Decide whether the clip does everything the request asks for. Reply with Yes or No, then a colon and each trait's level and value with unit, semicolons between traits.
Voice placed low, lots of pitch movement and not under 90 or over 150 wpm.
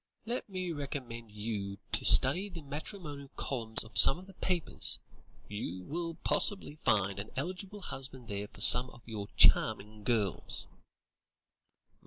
Yes: low, 130 Hz; wide, 8.2 semitones; average, 140 wpm